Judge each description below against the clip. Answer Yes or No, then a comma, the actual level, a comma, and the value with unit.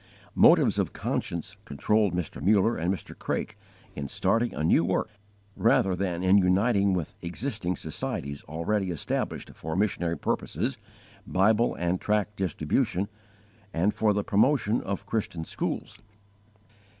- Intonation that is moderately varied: Yes, average, 3.6 semitones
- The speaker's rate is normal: No, slow, 130 wpm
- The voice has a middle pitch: No, very low, 95 Hz